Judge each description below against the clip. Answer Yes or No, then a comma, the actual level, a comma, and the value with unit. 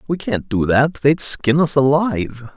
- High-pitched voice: No, medium, 140 Hz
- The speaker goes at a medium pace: Yes, average, 190 wpm